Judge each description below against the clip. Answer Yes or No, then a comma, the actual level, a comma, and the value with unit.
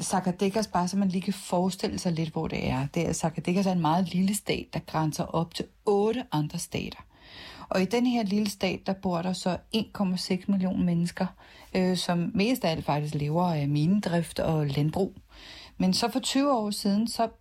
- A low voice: No, medium, 185 Hz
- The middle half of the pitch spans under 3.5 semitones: Yes, average, 3.1 semitones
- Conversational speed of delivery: Yes, average, 200 wpm